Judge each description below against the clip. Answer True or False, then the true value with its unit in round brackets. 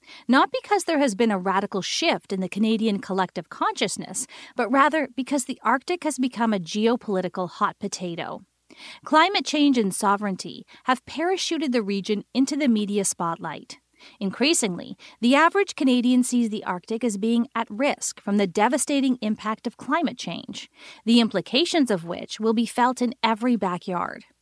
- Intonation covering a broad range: True (5.7 semitones)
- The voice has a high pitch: True (235 Hz)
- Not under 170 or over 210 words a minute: False (155 wpm)